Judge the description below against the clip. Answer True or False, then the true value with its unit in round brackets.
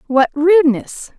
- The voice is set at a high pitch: True (305 Hz)